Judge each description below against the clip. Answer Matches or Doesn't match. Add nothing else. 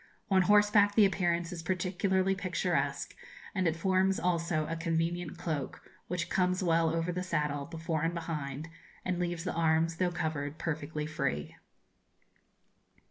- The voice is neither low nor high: Matches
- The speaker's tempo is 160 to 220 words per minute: Doesn't match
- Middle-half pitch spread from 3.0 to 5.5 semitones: Doesn't match